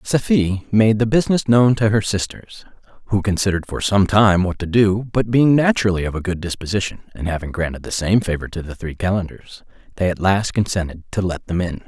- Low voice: Yes, low, 100 Hz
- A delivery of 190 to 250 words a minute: Yes, fast, 205 wpm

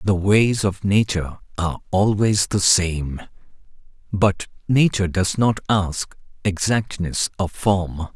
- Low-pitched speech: Yes, very low, 95 Hz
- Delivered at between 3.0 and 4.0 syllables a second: Yes, 3.8 syllables/s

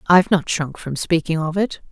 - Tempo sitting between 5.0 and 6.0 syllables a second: Yes, 5.3 syllables/s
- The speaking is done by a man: No, female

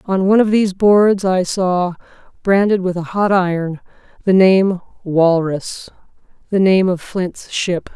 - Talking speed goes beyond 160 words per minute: No, average, 145 wpm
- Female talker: Yes, female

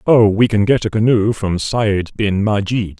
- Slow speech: No, average, 200 wpm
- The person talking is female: No, male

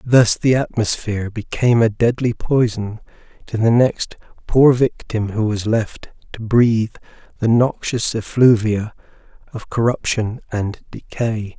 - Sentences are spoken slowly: Yes, slow, 125 wpm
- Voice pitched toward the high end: No, low, 115 Hz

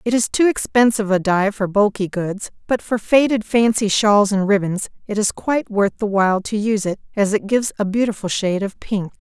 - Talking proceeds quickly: Yes, fast, 215 wpm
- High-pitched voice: Yes, high, 210 Hz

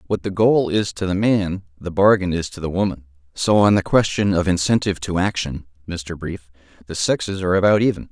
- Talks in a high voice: No, very low, 90 Hz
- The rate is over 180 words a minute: Yes, fast, 205 wpm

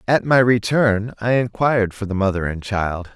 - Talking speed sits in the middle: Yes, average, 190 wpm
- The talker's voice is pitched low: Yes, low, 110 Hz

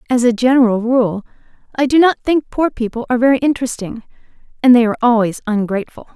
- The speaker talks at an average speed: Yes, average, 175 wpm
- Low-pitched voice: No, high, 240 Hz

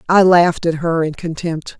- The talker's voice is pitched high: No, medium, 170 Hz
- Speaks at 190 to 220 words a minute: Yes, average, 200 wpm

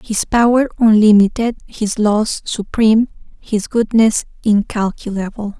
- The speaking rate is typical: No, slow, 95 wpm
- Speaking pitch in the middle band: No, high, 215 Hz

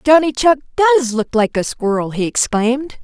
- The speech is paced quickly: No, average, 180 wpm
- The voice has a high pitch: Yes, very high, 255 Hz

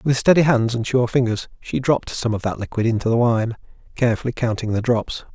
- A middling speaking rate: No, fast, 215 wpm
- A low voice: Yes, low, 120 Hz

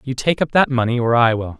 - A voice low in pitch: Yes, low, 125 Hz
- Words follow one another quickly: Yes, fast, 300 wpm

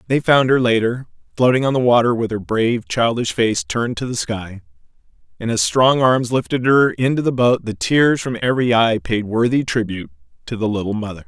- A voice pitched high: No, low, 115 Hz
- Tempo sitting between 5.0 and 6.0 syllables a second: Yes, 5.5 syllables/s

